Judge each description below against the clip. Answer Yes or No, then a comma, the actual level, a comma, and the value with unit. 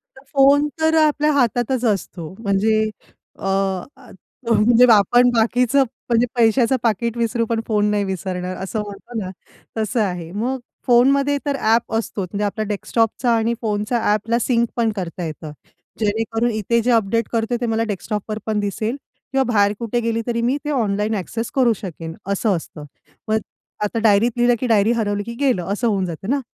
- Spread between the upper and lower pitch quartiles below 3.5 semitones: Yes, average, 2.8 semitones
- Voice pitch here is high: Yes, high, 225 Hz